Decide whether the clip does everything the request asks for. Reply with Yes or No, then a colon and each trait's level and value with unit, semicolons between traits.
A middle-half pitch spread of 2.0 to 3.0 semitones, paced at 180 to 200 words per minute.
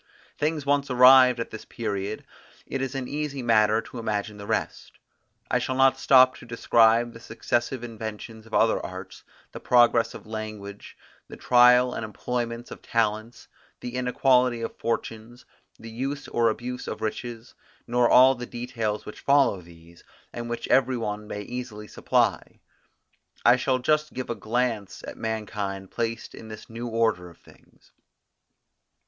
No: narrow, 2.5 semitones; average, 155 wpm